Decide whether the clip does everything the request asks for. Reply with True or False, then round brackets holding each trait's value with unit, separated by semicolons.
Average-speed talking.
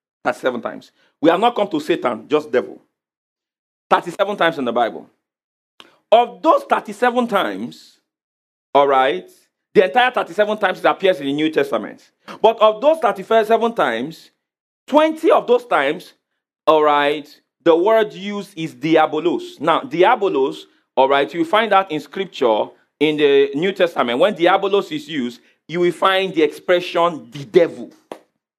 True (150 wpm)